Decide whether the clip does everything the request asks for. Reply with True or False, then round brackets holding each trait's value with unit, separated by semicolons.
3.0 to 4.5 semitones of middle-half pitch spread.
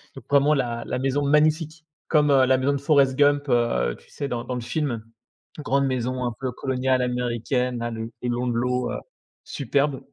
False (2.6 semitones)